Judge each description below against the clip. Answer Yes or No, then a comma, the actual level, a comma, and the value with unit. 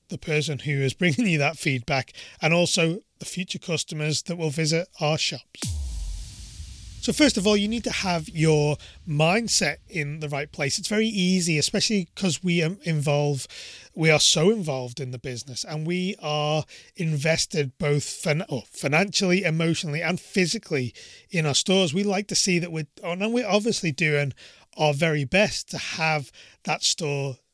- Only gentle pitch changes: No, average, 4.0 semitones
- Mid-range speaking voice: Yes, medium, 160 Hz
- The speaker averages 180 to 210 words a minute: No, average, 170 wpm